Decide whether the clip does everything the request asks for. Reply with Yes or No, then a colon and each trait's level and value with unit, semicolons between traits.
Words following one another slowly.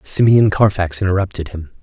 Yes: slow, 130 wpm